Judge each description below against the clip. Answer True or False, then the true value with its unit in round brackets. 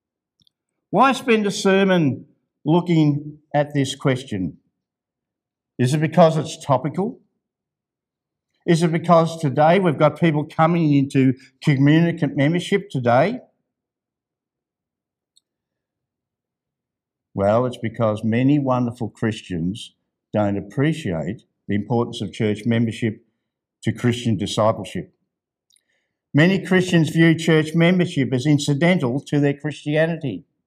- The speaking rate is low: True (100 wpm)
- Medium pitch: True (145 Hz)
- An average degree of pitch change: False (5.8 semitones)